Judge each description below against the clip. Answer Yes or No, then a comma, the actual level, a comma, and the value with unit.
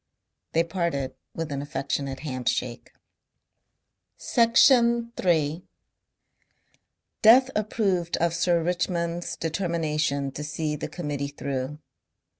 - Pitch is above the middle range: No, medium, 165 Hz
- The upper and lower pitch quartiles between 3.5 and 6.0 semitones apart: Yes, average, 3.9 semitones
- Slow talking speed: Yes, slow, 90 wpm